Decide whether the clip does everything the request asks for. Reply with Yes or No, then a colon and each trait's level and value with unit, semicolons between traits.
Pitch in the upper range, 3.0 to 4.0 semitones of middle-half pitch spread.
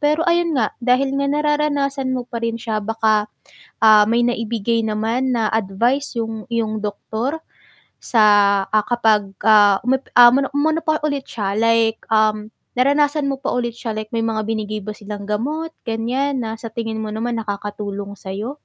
Yes: high, 230 Hz; average, 3.7 semitones